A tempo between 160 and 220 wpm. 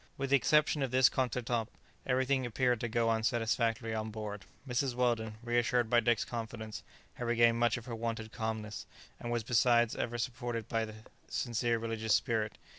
Yes: average, 175 wpm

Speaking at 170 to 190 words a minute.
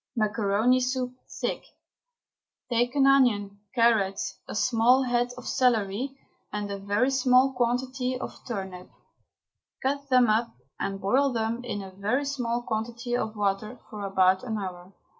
No: average, 140 wpm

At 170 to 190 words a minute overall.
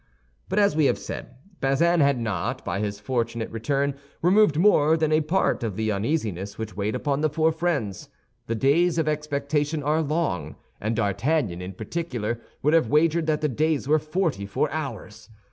Yes: average, 180 wpm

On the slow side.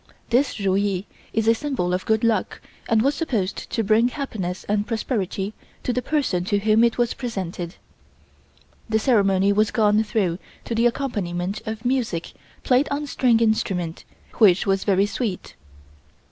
No: average, 160 wpm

